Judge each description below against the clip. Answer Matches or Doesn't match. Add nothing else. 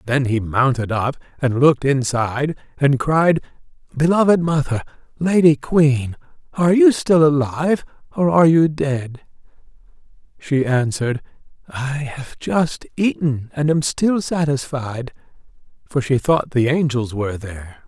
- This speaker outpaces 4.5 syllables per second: Doesn't match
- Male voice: Matches